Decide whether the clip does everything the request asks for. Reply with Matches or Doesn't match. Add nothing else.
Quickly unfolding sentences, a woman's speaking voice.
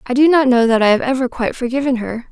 Matches